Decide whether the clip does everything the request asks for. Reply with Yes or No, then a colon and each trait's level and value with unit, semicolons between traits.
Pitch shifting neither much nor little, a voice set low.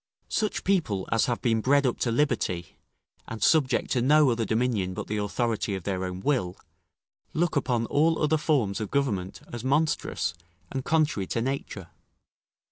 No: wide, 6.1 semitones; low, 120 Hz